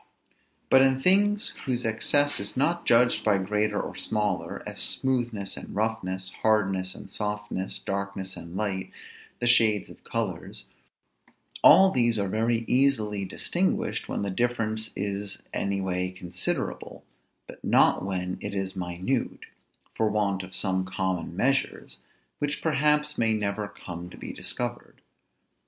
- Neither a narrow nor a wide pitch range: Yes, average, 4.3 semitones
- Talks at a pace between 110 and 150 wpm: Yes, average, 140 wpm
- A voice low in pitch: Yes, low, 105 Hz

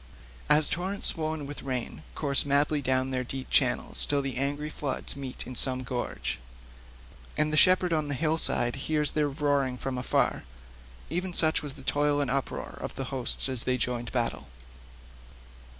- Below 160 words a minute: No, average, 165 wpm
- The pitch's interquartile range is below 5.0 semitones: Yes, average, 2.9 semitones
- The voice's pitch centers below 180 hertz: Yes, medium, 140 Hz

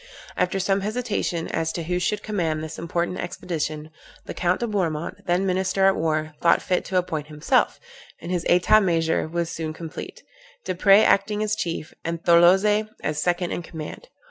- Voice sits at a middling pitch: Yes, medium, 175 Hz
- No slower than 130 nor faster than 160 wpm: No, average, 170 wpm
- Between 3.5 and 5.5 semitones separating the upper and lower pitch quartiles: No, average, 2.9 semitones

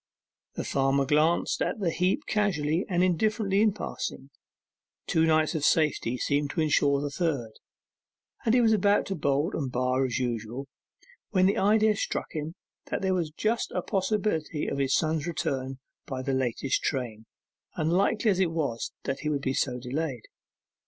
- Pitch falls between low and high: Yes, medium, 155 Hz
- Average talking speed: Yes, average, 170 wpm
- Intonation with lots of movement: Yes, wide, 5.8 semitones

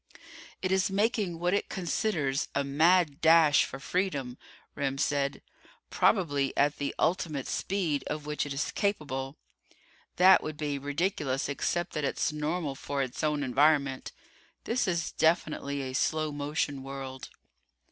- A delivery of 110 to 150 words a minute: Yes, average, 140 wpm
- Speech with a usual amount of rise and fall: Yes, average, 3.8 semitones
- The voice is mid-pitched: Yes, medium, 150 Hz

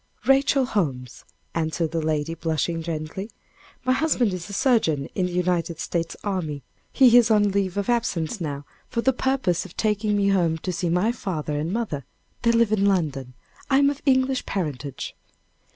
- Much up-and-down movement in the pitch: Yes, wide, 6.4 semitones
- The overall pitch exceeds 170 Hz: Yes, medium, 185 Hz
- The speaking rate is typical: Yes, average, 175 wpm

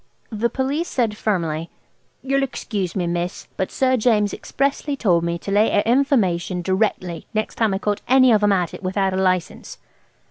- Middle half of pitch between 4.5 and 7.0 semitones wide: Yes, average, 5.1 semitones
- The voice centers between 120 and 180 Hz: No, high, 205 Hz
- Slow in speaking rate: No, average, 180 wpm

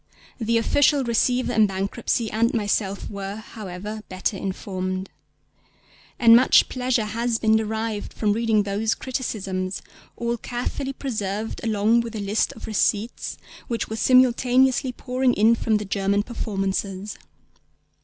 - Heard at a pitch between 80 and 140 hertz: No, high, 220 Hz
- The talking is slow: Yes, slow, 130 wpm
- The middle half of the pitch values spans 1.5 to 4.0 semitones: Yes, average, 2.9 semitones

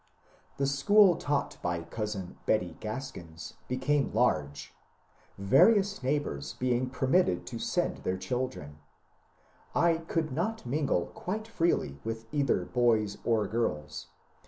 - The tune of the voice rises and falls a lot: Yes, wide, 7.3 semitones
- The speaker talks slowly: Yes, slow, 115 wpm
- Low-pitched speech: Yes, low, 125 Hz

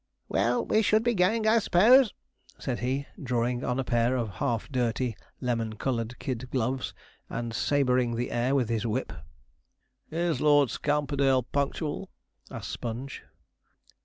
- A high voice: No, low, 130 Hz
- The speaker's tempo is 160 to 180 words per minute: No, average, 140 wpm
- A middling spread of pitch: Yes, average, 3.5 semitones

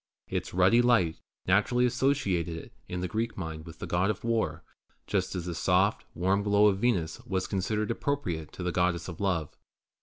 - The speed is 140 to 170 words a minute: No, average, 185 wpm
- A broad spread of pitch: No, average, 3.8 semitones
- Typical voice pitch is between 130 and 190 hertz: No, very low, 95 Hz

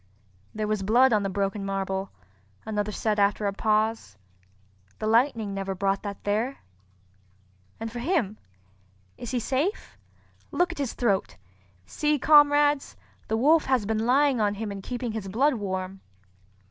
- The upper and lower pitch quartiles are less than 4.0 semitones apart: No, average, 4.5 semitones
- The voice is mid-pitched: No, high, 215 Hz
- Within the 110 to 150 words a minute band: Yes, average, 145 wpm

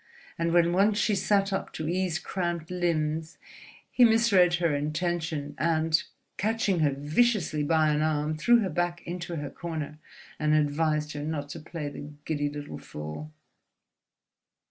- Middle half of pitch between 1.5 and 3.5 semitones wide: Yes, average, 2.8 semitones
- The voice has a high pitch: No, medium, 160 Hz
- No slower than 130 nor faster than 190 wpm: Yes, average, 150 wpm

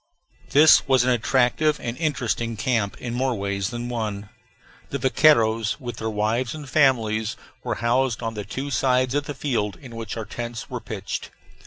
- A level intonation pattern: No, average, 3.0 semitones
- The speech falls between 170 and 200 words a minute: Yes, average, 175 wpm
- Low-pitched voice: Yes, low, 120 Hz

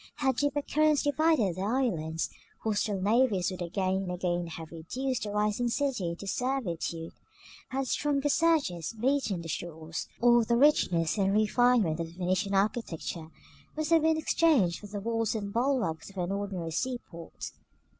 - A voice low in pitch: No, high, 210 Hz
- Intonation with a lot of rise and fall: Yes, wide, 7.0 semitones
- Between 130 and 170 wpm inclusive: Yes, average, 160 wpm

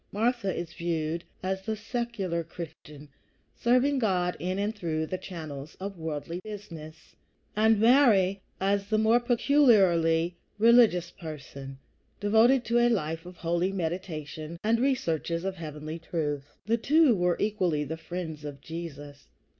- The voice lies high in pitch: No, medium, 180 Hz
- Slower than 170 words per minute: Yes, average, 140 wpm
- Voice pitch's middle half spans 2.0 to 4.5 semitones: No, average, 5.2 semitones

